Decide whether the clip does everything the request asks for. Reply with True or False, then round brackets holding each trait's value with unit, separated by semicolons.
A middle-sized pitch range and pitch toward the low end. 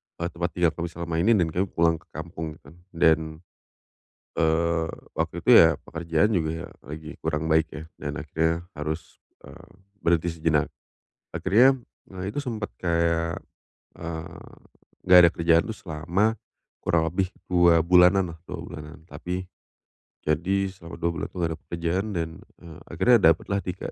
False (1.9 semitones; 85 Hz)